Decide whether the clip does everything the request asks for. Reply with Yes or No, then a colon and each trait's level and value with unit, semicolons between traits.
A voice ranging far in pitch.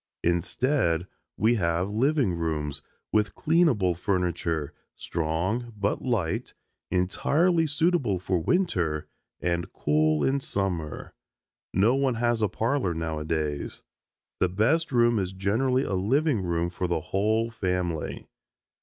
Yes: wide, 6.2 semitones